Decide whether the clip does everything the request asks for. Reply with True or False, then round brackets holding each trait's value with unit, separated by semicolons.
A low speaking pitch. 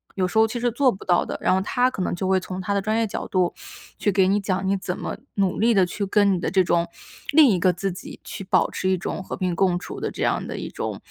False (190 Hz)